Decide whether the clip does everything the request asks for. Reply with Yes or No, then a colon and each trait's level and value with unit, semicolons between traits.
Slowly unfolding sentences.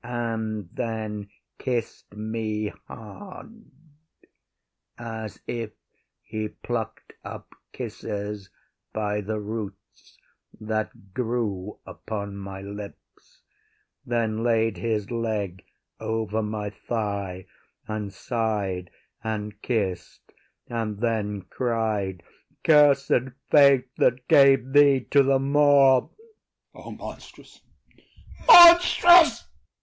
Yes: slow, 95 wpm